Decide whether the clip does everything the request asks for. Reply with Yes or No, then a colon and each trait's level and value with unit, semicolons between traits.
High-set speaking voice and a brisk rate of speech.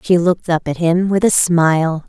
No: medium, 170 Hz; fast, 230 wpm